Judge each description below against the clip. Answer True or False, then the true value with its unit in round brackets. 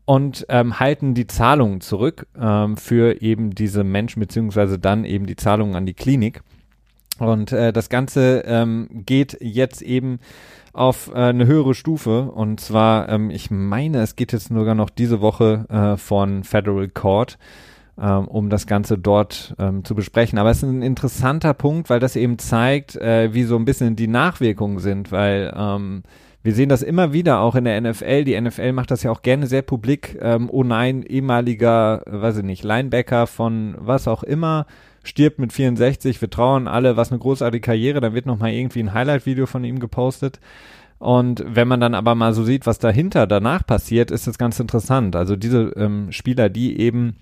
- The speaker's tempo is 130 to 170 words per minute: False (185 wpm)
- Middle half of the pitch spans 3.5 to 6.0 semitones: False (3.0 semitones)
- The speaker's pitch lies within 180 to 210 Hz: False (115 Hz)